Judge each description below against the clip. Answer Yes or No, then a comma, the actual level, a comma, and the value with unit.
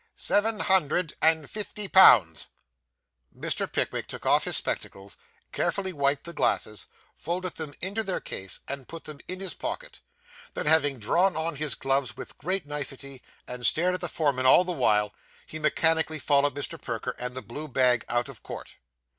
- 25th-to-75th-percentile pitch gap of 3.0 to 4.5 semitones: No, average, 5.3 semitones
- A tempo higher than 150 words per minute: Yes, average, 170 wpm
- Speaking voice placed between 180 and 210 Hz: No, medium, 150 Hz